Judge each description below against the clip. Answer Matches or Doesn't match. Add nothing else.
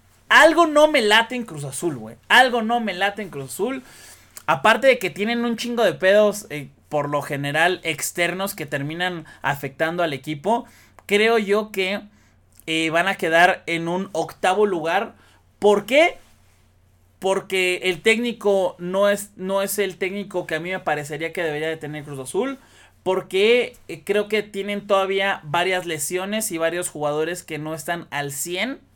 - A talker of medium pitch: Matches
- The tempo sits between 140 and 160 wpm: Doesn't match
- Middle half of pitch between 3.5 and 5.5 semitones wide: Matches